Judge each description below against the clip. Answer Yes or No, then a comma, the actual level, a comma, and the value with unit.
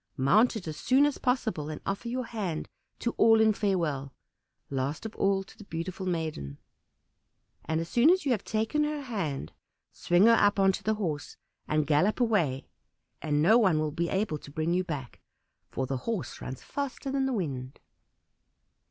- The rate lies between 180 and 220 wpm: Yes, average, 185 wpm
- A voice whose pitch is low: No, medium, 185 Hz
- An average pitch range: No, wide, 6.8 semitones